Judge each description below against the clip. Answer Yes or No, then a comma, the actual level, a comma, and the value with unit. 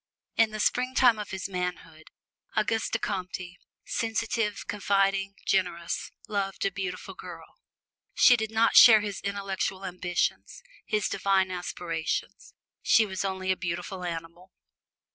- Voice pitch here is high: Yes, high, 195 Hz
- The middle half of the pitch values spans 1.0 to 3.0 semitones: Yes, narrow, 2.6 semitones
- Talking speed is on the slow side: Yes, slow, 125 wpm